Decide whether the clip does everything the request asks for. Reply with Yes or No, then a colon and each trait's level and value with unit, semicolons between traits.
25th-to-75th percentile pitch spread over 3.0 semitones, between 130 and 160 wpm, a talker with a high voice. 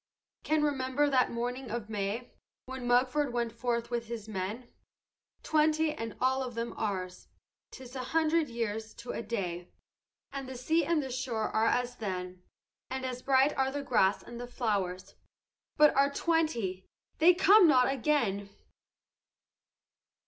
Yes: average, 3.9 semitones; average, 150 wpm; high, 245 Hz